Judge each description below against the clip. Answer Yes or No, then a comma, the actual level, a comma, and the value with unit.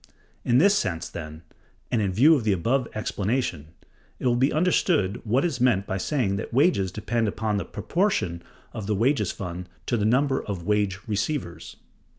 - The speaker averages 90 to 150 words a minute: No, average, 180 wpm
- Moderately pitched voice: No, low, 110 Hz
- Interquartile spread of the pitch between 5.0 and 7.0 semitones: Yes, wide, 5.6 semitones